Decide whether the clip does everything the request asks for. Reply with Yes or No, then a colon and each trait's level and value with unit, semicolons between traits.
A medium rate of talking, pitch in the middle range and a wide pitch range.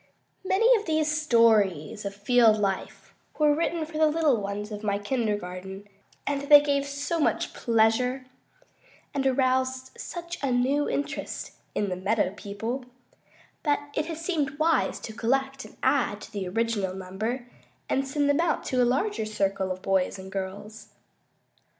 No: average, 155 wpm; high, 245 Hz; wide, 6.0 semitones